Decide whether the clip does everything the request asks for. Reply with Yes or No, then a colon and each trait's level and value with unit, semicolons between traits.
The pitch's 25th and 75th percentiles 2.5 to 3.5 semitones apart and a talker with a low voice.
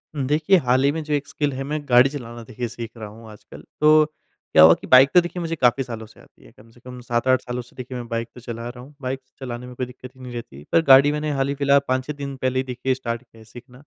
Yes: average, 2.8 semitones; low, 130 Hz